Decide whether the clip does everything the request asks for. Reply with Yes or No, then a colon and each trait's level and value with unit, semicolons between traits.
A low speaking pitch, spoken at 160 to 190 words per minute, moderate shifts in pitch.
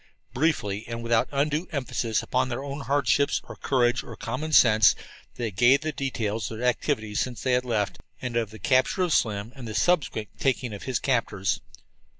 Yes: low, 120 Hz; average, 185 wpm; average, 3.8 semitones